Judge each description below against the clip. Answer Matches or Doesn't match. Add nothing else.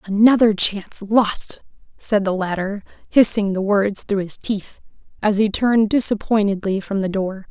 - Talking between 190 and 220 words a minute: Doesn't match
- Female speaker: Matches